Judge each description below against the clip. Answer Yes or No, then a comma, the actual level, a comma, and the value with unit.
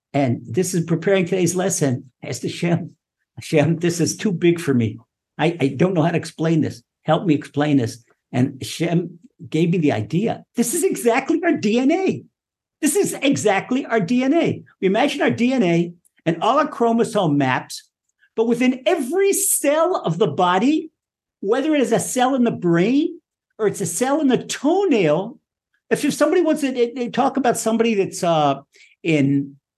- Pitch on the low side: No, high, 190 Hz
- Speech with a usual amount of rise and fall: No, wide, 8.8 semitones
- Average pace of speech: Yes, average, 175 wpm